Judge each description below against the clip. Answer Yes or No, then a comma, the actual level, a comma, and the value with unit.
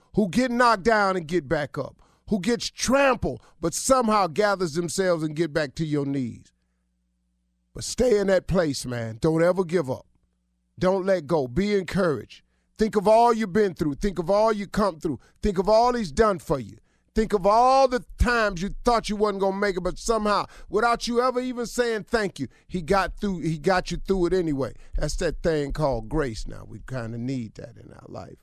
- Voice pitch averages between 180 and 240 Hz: Yes, medium, 185 Hz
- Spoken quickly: Yes, fast, 210 wpm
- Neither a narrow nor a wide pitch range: No, wide, 6.8 semitones